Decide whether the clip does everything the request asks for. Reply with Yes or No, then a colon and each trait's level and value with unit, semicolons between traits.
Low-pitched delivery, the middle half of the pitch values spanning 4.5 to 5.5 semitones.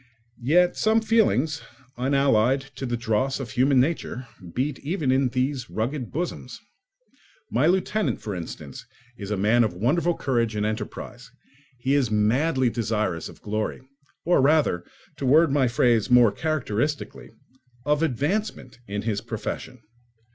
Yes: low, 130 Hz; average, 4.9 semitones